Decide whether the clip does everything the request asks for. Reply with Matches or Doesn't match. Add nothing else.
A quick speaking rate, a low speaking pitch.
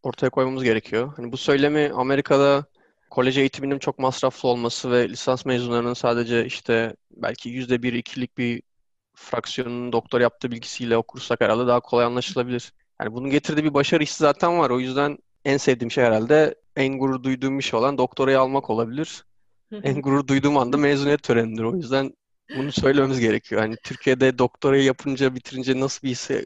Matches